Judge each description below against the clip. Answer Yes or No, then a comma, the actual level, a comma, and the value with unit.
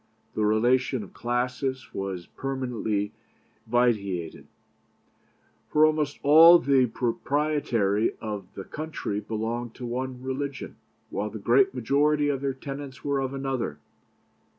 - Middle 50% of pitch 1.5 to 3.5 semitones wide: No, average, 4.2 semitones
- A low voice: Yes, low, 130 Hz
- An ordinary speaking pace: No, slow, 120 wpm